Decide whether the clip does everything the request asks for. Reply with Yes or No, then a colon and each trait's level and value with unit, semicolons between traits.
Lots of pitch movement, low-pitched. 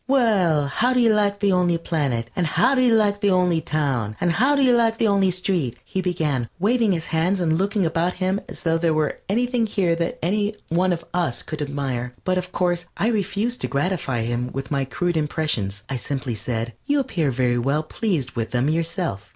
No: wide, 6.3 semitones; medium, 170 Hz